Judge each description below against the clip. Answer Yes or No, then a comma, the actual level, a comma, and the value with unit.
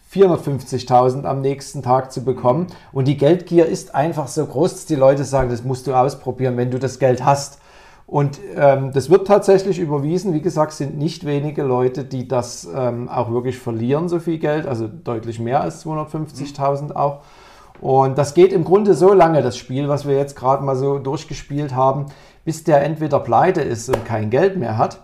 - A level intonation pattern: No, average, 3.3 semitones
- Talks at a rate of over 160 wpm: Yes, fast, 190 wpm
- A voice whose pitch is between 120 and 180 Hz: Yes, medium, 140 Hz